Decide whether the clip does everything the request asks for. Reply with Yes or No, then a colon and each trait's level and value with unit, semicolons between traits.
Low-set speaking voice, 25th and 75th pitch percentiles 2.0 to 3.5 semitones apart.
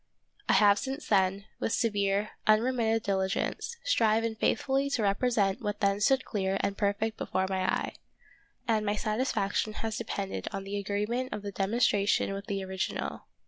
No: high, 210 Hz; narrow, 2.4 semitones